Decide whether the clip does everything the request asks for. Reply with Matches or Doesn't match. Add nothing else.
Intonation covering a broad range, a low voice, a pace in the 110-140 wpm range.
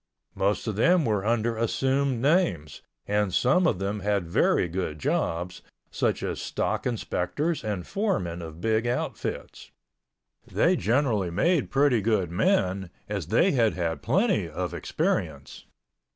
Matches